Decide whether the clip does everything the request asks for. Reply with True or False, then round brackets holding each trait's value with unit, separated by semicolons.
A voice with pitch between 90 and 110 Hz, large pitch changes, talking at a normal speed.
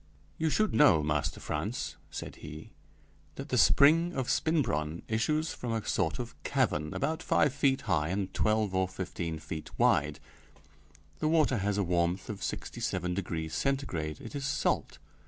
True (105 Hz; 8.6 semitones; 160 wpm)